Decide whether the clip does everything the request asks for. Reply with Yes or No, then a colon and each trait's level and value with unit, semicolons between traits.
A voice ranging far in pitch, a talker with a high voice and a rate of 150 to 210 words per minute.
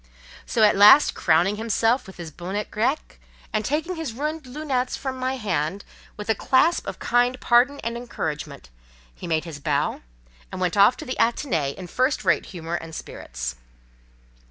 Yes: wide, 7.1 semitones; high, 215 Hz; average, 170 wpm